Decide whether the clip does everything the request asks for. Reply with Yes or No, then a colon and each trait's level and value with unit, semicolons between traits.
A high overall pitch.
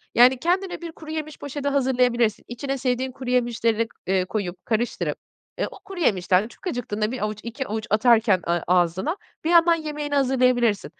Yes: high, 245 Hz